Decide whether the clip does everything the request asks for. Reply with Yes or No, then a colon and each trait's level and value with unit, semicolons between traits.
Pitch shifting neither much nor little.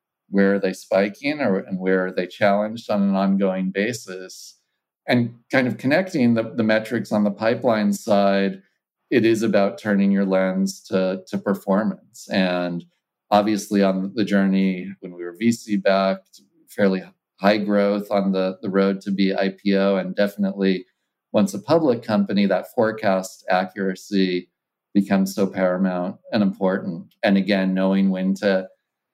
No: narrow, 1.3 semitones